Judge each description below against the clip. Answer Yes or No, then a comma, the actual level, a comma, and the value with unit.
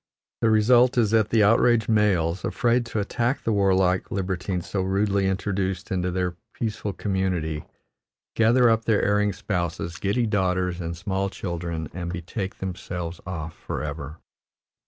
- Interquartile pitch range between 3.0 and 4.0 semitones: Yes, average, 3.4 semitones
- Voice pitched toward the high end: No, very low, 95 Hz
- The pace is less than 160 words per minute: Yes, average, 140 wpm